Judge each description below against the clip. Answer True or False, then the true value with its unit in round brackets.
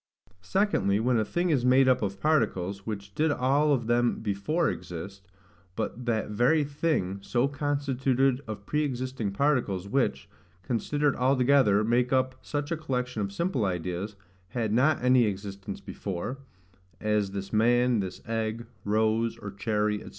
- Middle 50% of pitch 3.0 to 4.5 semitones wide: False (5.0 semitones)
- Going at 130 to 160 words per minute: True (155 wpm)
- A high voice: False (120 Hz)